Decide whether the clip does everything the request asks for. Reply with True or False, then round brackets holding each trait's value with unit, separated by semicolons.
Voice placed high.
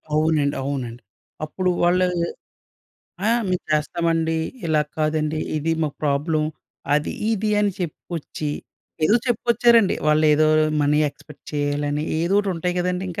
False (155 Hz)